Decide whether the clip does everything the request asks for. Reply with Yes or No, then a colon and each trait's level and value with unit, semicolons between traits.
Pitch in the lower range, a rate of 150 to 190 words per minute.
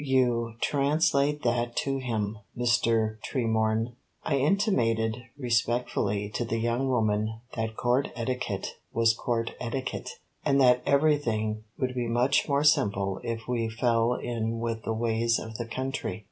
No: low, 120 Hz; average, 140 wpm